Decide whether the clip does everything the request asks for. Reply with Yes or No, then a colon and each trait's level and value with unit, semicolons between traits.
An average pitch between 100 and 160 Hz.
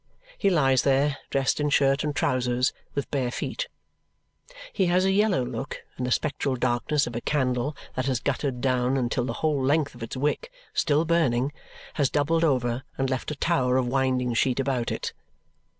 Yes: low, 135 Hz